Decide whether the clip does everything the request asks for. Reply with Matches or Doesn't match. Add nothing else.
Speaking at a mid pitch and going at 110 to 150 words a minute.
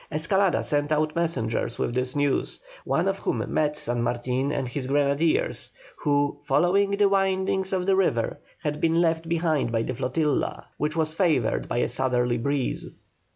Doesn't match